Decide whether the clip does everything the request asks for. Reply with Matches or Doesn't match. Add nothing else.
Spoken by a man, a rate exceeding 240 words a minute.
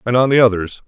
Matches